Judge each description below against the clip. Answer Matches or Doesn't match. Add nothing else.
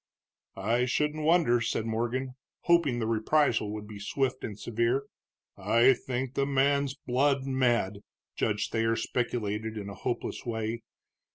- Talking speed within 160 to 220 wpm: Doesn't match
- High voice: Doesn't match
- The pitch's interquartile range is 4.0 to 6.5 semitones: Doesn't match